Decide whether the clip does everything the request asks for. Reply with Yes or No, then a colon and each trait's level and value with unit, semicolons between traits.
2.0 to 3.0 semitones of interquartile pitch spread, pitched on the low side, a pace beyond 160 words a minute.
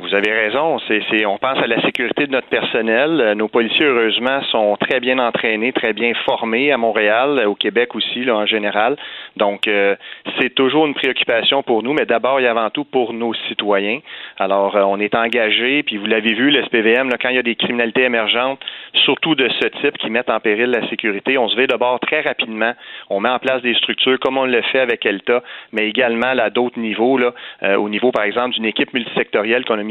Yes: average, 2.7 semitones; low, 115 Hz; average, 215 wpm